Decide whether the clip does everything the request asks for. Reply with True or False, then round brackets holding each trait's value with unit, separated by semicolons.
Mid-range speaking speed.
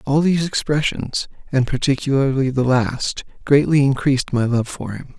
True (150 wpm)